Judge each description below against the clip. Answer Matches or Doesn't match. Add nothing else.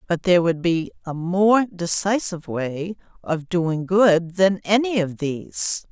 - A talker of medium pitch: Matches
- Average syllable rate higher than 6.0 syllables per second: Doesn't match